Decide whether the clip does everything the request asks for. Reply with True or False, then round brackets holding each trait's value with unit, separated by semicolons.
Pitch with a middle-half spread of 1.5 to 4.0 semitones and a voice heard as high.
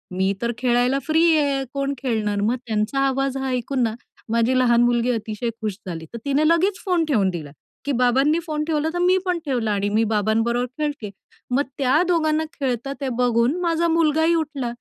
False (4.8 semitones; 260 Hz)